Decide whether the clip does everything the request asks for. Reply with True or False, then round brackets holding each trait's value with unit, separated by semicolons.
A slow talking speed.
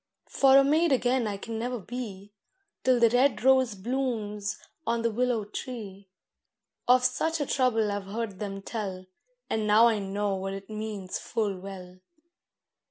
False (160 wpm)